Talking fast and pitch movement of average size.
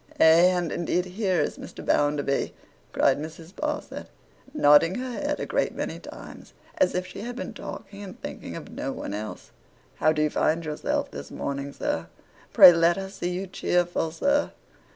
No: average, 175 wpm; average, 4.0 semitones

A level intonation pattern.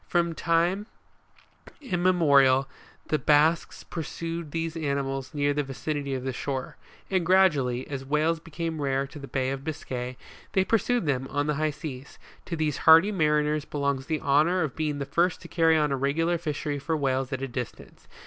No: average, 3.2 semitones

